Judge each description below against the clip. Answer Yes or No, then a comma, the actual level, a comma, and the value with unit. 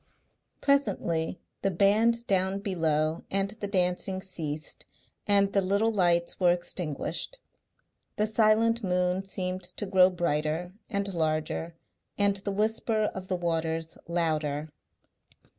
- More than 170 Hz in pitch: Yes, medium, 185 Hz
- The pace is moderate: No, slow, 120 wpm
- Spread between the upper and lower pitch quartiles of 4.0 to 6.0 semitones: No, average, 3.2 semitones